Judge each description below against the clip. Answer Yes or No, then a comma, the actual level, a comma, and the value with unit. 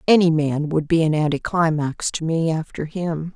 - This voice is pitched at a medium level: Yes, medium, 160 Hz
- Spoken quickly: No, average, 180 wpm